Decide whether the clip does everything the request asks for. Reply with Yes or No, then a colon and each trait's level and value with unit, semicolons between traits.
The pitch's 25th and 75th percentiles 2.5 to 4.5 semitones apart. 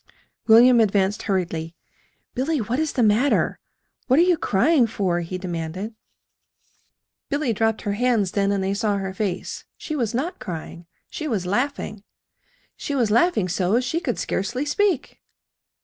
No: wide, 5.4 semitones